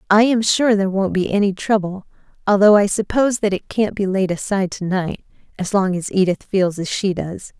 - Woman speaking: Yes, female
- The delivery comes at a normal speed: No, fast, 215 wpm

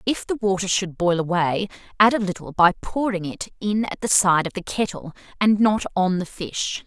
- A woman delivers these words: Yes, female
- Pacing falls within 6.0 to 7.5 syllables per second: No, 4.9 syllables/s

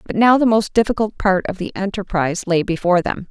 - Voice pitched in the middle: No, high, 195 Hz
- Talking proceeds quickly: Yes, fast, 220 wpm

